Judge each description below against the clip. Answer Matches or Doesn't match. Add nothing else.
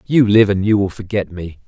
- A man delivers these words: Matches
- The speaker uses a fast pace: Matches